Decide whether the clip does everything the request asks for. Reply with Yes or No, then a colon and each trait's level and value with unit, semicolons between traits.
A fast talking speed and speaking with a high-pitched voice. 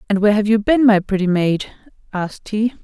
Yes: fast, 210 wpm; high, 205 Hz